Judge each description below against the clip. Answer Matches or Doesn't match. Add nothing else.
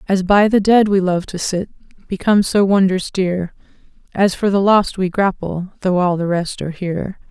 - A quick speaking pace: Doesn't match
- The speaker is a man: Doesn't match